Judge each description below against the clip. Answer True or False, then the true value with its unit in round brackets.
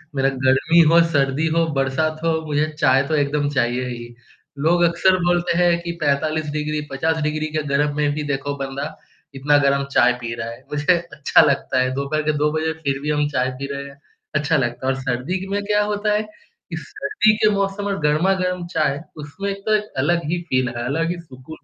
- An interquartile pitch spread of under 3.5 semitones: False (3.9 semitones)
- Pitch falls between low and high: True (150 Hz)